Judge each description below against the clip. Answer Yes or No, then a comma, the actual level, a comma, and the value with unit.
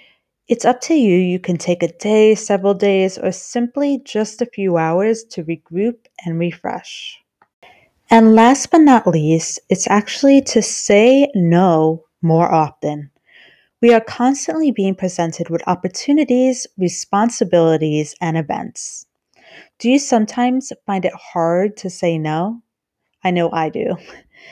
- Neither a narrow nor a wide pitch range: No, wide, 5.8 semitones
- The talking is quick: No, slow, 135 wpm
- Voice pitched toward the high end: Yes, high, 195 Hz